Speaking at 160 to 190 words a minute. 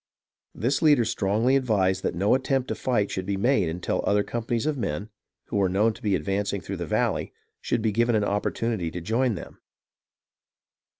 Yes: average, 185 wpm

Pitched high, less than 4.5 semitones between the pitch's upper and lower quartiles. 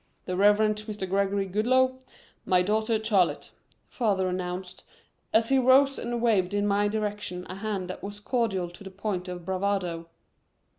Yes: high, 200 Hz; average, 2.8 semitones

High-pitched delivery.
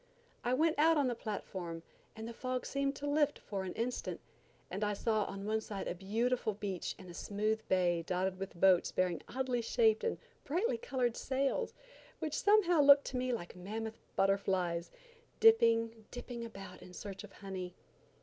Yes: high, 220 Hz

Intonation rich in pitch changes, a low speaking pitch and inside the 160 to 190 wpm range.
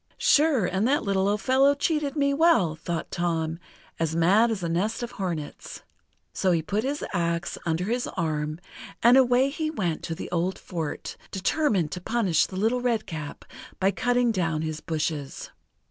No: wide, 6.9 semitones; high, 190 Hz; average, 170 wpm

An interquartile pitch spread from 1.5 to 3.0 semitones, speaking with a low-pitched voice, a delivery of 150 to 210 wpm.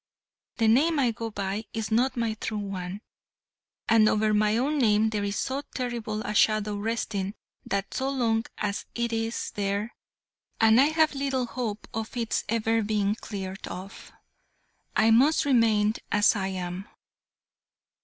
No: narrow, 2.4 semitones; high, 220 Hz; average, 155 wpm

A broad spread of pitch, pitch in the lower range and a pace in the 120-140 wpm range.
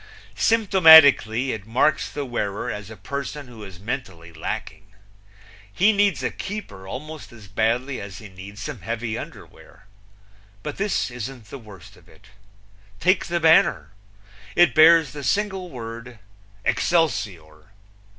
Yes: wide, 7.6 semitones; low, 120 Hz; slow, 135 wpm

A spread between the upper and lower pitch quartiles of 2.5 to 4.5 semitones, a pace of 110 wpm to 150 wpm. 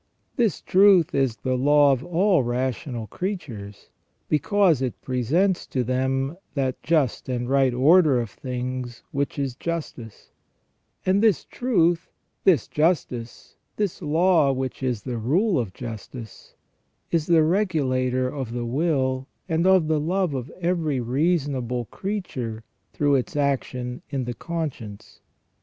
No: average, 5.2 semitones; slow, 135 wpm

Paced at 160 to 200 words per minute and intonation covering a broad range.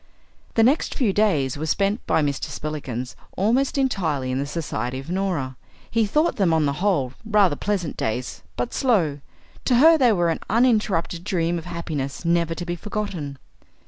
Yes: average, 175 wpm; wide, 6.5 semitones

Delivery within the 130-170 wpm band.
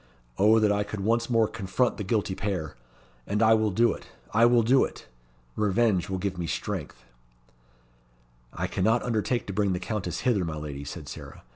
No: average, 185 wpm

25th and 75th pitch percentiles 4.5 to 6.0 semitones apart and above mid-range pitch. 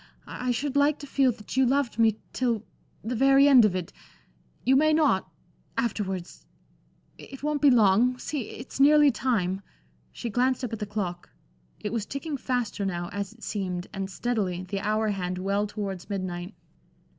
Yes: average, 5.2 semitones; high, 220 Hz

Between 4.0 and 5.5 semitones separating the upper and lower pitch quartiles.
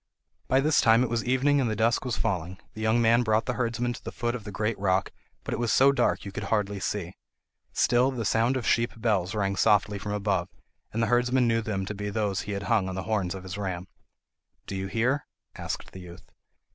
No: average, 3.4 semitones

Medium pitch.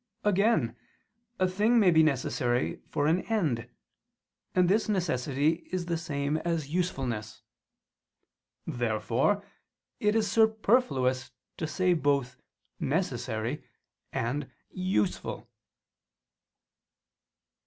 Yes: medium, 160 Hz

